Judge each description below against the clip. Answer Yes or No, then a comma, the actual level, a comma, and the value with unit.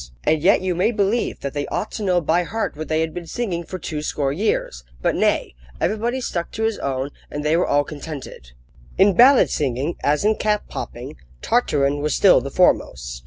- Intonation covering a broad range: Yes, wide, 6.2 semitones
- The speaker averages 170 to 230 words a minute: Yes, average, 200 wpm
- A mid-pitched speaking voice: Yes, medium, 165 Hz